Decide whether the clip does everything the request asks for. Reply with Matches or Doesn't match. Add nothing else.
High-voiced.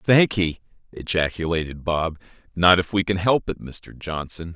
Doesn't match